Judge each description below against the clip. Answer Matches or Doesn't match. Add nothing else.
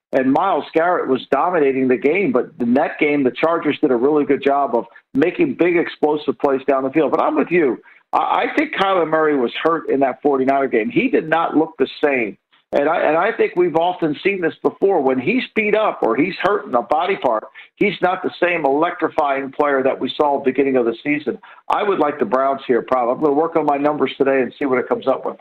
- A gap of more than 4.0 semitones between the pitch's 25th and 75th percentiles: Doesn't match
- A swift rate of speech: Matches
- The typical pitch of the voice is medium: Matches